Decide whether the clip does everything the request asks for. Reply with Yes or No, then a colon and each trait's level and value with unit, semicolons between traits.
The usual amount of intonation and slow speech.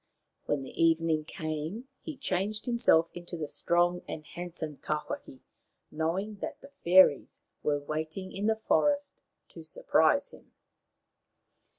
Yes: average, 5.0 semitones; slow, 125 wpm